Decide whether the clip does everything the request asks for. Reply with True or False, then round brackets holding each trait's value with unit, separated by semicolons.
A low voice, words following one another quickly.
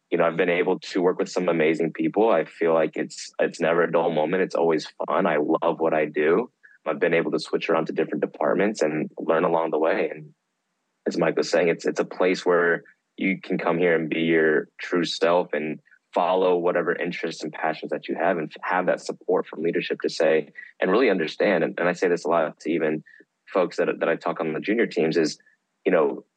True (85 Hz; 235 wpm)